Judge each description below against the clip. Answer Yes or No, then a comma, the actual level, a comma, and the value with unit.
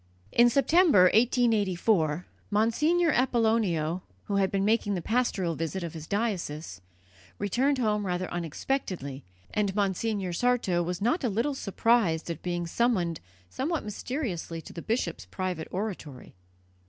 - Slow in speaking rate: Yes, slow, 130 wpm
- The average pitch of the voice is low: No, high, 200 Hz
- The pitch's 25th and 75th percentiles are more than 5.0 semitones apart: Yes, wide, 5.4 semitones